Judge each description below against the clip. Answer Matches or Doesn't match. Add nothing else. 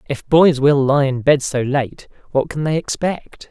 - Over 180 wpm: Matches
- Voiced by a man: Matches